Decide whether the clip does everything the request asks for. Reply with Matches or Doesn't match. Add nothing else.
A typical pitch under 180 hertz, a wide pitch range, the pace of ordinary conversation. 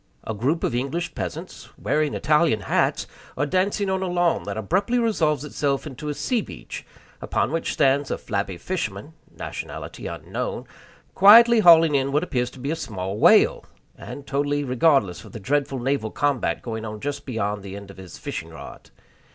Matches